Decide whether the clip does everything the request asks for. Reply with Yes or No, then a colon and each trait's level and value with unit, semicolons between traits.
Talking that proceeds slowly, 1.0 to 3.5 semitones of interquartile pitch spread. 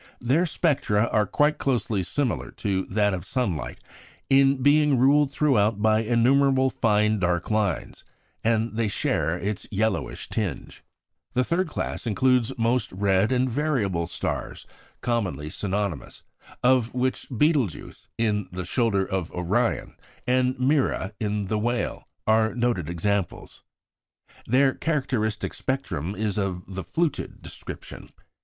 No: slow, 125 wpm; average, 4.8 semitones